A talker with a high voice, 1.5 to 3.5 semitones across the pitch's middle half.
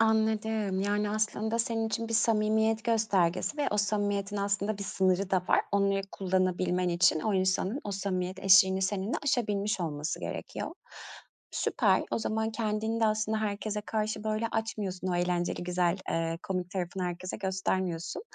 Yes: high, 200 Hz; average, 2.8 semitones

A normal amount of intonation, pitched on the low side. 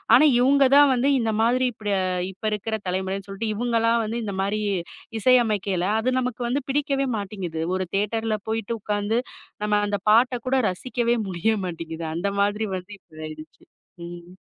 No: average, 3.9 semitones; high, 215 Hz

